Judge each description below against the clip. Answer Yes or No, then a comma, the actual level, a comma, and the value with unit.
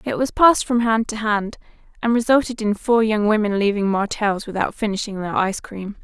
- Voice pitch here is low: No, high, 215 Hz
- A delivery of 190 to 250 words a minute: Yes, average, 200 wpm